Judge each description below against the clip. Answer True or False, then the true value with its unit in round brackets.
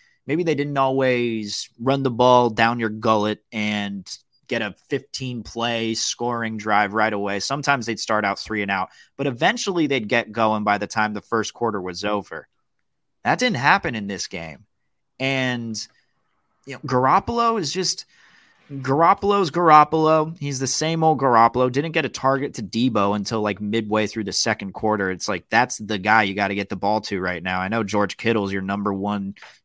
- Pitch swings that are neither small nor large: True (4.6 semitones)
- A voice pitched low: True (115 Hz)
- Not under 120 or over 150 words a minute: False (185 wpm)